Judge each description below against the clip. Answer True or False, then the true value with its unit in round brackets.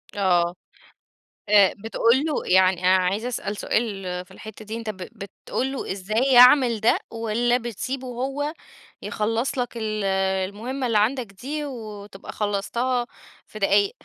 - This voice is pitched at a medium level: False (220 Hz)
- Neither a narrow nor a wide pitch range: True (3.7 semitones)